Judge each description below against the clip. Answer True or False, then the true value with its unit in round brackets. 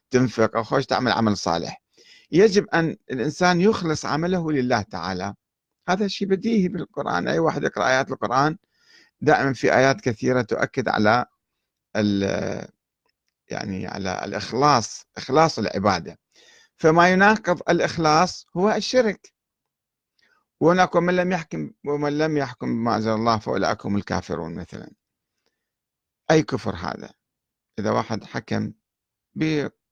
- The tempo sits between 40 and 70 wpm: False (115 wpm)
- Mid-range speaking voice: True (145 Hz)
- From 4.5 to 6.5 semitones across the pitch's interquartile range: False (8.2 semitones)